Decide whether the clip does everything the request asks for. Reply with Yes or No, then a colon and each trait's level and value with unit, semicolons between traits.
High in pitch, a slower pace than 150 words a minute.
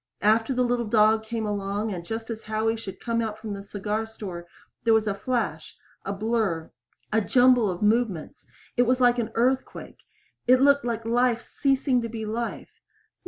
No: high, 225 Hz; average, 180 wpm